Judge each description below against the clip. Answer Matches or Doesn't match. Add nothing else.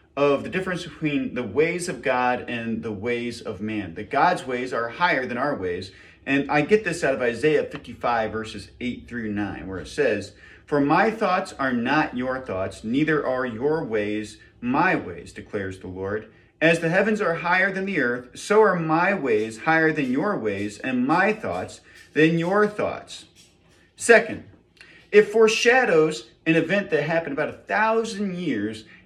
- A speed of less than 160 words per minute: Doesn't match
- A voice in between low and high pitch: Matches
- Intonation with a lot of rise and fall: Matches